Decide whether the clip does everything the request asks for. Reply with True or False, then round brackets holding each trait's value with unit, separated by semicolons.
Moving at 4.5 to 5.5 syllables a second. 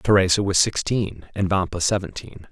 True (5.0 syllables/s)